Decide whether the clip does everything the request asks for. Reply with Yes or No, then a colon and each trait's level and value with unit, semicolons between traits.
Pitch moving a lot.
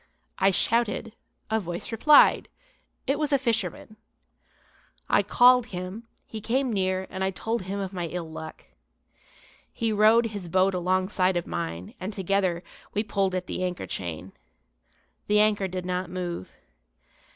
No: average, 3.4 semitones